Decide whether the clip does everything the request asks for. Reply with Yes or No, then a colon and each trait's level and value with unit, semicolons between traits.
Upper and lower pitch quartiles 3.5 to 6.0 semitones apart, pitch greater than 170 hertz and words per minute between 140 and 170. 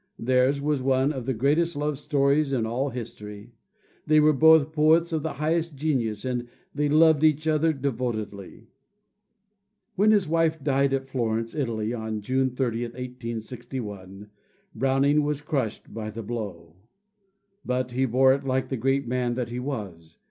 No: average, 4.2 semitones; low, 130 Hz; average, 155 wpm